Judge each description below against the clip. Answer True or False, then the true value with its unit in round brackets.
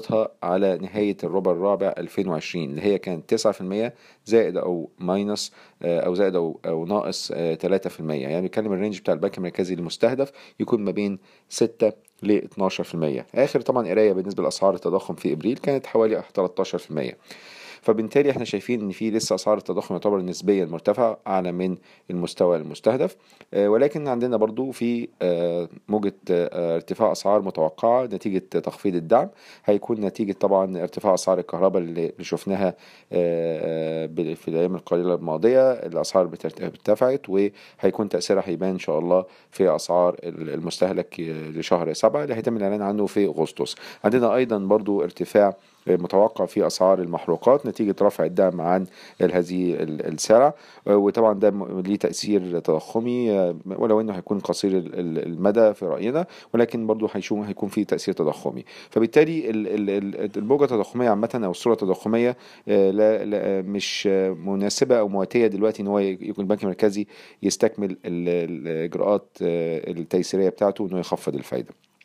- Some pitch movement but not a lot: True (3.0 semitones)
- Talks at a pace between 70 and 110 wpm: False (130 wpm)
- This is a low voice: True (100 Hz)